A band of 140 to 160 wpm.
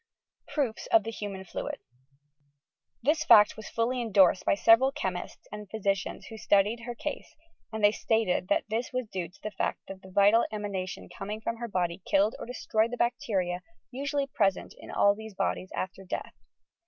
No: average, 180 wpm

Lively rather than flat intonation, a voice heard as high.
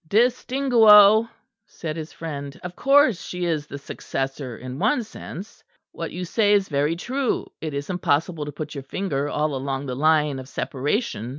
No: wide, 6.7 semitones; medium, 160 Hz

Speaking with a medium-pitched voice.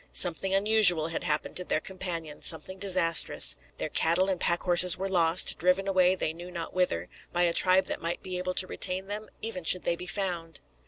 Yes: medium, 180 Hz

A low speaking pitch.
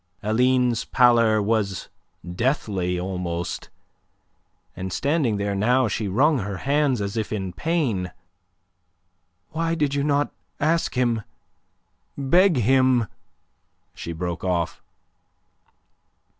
Yes: low, 115 Hz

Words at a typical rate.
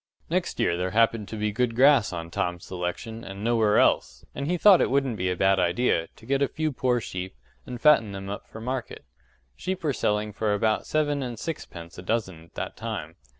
No: fast, 215 wpm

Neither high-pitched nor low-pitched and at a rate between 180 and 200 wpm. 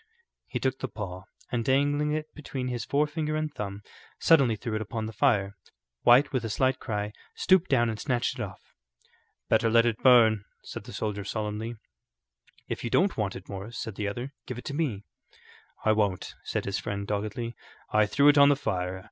No: low, 115 Hz; average, 195 wpm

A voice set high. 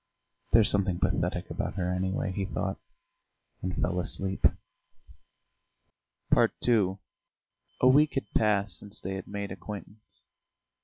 No: very low, 95 Hz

